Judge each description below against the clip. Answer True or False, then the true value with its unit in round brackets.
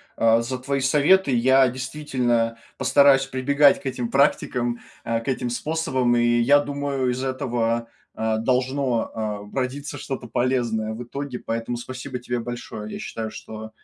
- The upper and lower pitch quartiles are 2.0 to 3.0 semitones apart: True (2.6 semitones)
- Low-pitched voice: True (125 Hz)